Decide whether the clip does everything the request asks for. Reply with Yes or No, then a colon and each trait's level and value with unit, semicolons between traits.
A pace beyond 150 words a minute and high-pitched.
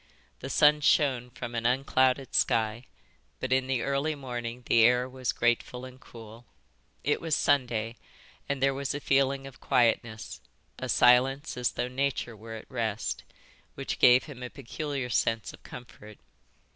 No: average, 160 wpm; low, 125 Hz